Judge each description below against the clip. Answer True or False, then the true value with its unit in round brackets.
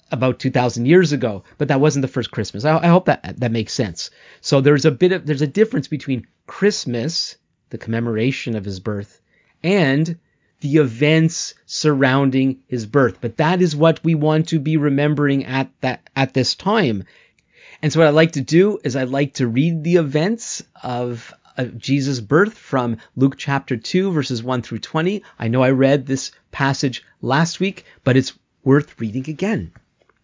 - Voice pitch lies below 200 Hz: True (140 Hz)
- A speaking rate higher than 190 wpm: False (180 wpm)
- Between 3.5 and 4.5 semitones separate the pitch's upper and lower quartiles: True (3.9 semitones)